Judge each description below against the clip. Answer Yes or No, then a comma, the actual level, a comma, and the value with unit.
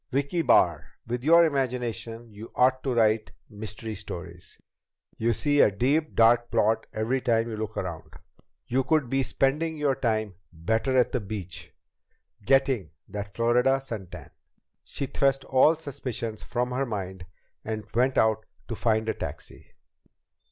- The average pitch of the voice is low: Yes, low, 120 Hz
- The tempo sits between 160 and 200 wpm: No, average, 150 wpm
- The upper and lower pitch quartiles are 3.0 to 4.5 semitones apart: Yes, average, 3.7 semitones